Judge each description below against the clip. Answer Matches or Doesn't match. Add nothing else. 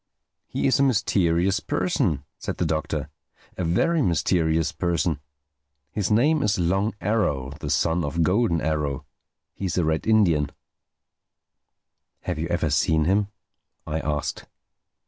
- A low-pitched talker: Matches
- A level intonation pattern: Doesn't match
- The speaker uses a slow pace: Matches